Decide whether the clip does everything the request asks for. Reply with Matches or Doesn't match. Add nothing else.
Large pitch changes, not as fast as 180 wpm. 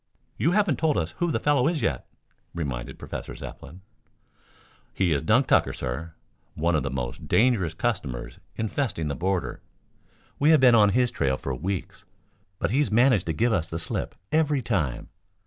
Matches